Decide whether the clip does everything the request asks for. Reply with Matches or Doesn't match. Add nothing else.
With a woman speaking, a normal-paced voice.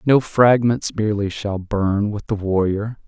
Doesn't match